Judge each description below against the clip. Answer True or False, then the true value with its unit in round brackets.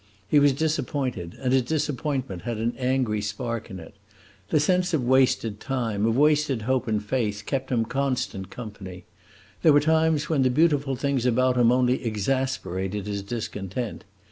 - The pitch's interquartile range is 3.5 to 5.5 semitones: True (4.5 semitones)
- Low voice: True (125 Hz)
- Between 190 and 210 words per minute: False (165 wpm)